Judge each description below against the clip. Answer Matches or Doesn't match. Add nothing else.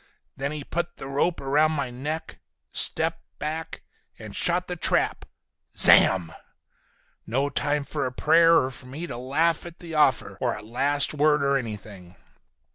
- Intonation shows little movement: Doesn't match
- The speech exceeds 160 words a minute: Doesn't match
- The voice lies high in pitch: Doesn't match